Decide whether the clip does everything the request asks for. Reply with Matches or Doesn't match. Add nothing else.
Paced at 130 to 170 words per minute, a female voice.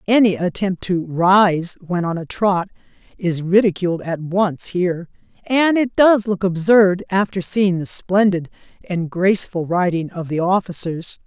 Matches